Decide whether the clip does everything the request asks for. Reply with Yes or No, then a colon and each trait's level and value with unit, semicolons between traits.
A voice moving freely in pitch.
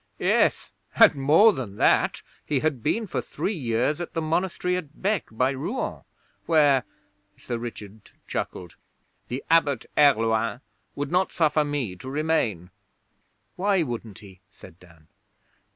Yes: wide, 6.4 semitones